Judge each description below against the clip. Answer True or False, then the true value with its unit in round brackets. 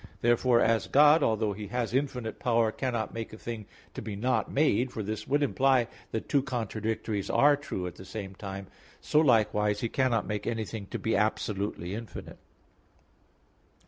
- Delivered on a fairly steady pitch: False (3.3 semitones)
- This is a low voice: True (115 Hz)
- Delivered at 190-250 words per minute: False (170 wpm)